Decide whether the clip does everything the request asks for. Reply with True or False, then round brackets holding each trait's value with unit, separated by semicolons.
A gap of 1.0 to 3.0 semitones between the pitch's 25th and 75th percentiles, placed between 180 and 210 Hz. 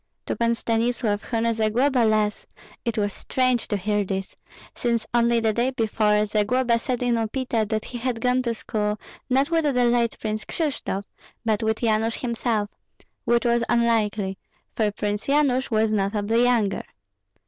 False (2.4 semitones; 230 Hz)